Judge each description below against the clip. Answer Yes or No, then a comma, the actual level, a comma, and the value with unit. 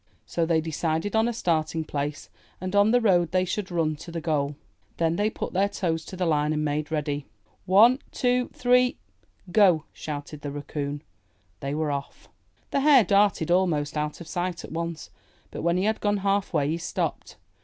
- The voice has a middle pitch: Yes, medium, 170 Hz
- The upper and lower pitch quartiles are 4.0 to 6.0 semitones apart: Yes, average, 4.7 semitones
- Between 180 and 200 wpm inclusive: Yes, average, 190 wpm